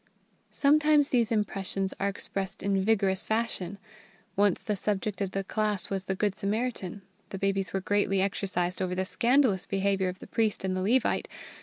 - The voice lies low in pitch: No, high, 195 Hz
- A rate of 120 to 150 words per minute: No, average, 170 wpm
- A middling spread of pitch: No, narrow, 2.1 semitones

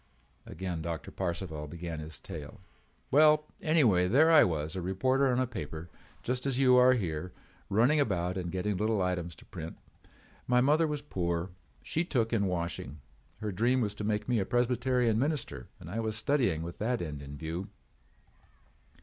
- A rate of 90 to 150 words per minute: No, average, 175 wpm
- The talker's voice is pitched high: No, low, 105 Hz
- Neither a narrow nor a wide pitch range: No, wide, 6.6 semitones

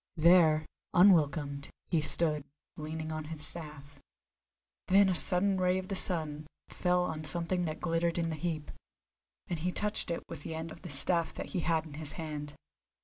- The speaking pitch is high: No, medium, 160 Hz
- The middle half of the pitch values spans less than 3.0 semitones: Yes, narrow, 2.5 semitones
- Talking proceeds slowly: No, average, 180 wpm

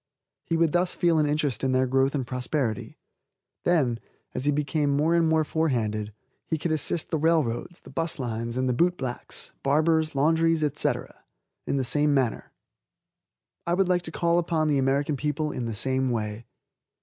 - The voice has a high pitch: No, medium, 145 Hz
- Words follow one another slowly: No, average, 180 wpm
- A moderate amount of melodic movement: Yes, average, 3.9 semitones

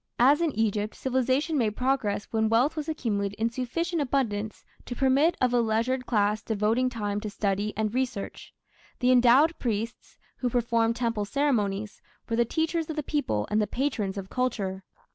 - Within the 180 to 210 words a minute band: No, average, 170 wpm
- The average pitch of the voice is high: Yes, high, 235 Hz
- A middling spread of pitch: Yes, average, 3.8 semitones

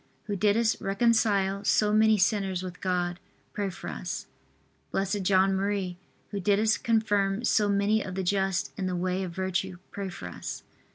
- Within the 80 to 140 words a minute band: No, average, 165 wpm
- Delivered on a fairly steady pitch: Yes, narrow, 1.9 semitones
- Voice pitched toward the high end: Yes, high, 195 Hz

